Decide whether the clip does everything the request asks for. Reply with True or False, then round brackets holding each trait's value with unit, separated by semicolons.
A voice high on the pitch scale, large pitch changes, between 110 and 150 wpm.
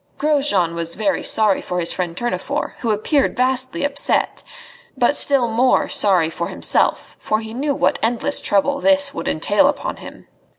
False (240 Hz; 6.3 semitones; 165 wpm)